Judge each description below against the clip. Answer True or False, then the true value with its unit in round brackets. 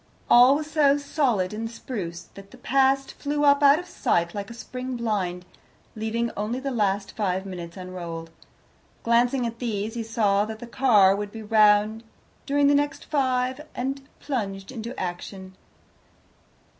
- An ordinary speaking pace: True (155 wpm)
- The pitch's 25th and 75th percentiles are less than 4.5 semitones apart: False (5.0 semitones)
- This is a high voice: True (230 Hz)